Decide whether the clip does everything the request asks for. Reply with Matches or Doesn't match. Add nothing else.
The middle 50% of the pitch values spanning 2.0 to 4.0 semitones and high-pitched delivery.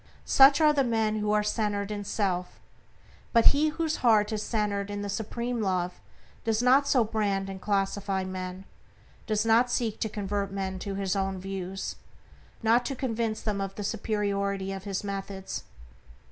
Matches